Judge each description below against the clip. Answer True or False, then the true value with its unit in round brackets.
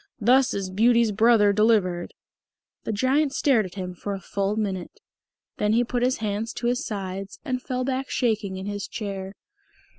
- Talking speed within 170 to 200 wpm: True (175 wpm)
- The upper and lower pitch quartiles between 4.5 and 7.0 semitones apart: False (3.7 semitones)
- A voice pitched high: True (215 Hz)